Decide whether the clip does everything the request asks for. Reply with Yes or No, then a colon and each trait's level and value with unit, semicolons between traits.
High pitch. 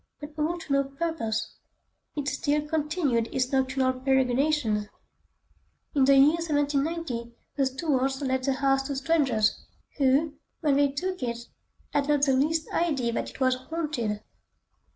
Yes: very high, 275 Hz